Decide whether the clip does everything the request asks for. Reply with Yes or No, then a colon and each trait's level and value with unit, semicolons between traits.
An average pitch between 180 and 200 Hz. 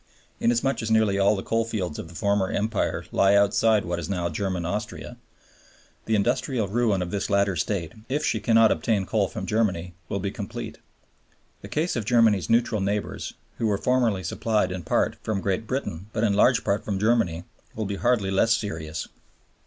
No: low, 105 Hz